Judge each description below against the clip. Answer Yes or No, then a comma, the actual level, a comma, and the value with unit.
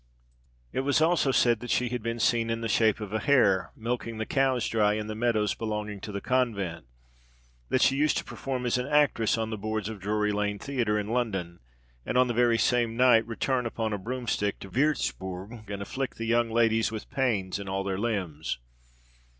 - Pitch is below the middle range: Yes, low, 115 Hz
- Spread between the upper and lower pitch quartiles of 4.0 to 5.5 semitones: No, average, 3.0 semitones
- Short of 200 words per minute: No, fast, 205 wpm